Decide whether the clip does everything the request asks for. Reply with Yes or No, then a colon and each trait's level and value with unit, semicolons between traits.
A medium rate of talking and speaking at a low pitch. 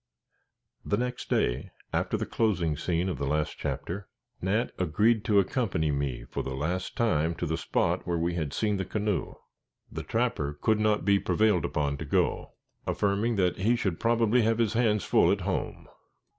Yes: average, 180 wpm; very low, 95 Hz